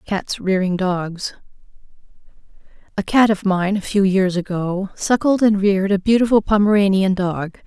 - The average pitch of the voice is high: Yes, high, 195 Hz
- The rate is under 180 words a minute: Yes, slow, 135 wpm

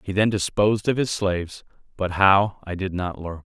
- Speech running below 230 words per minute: Yes, fast, 205 wpm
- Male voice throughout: Yes, male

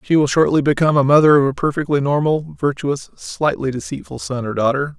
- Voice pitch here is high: No, medium, 145 Hz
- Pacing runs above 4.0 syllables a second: Yes, 5.8 syllables/s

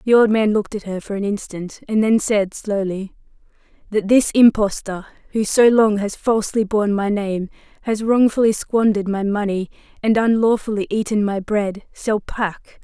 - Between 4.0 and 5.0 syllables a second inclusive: Yes, 4.9 syllables/s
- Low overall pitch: No, high, 210 Hz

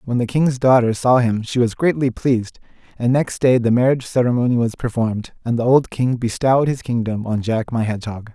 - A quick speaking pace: Yes, fast, 210 wpm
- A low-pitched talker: Yes, low, 120 Hz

